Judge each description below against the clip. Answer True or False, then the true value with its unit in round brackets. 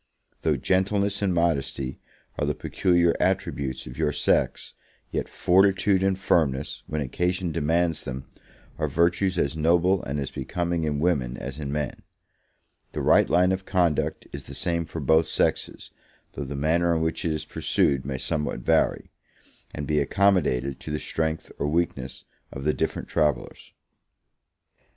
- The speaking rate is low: False (155 wpm)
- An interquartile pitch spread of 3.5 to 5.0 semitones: True (3.8 semitones)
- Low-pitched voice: True (80 Hz)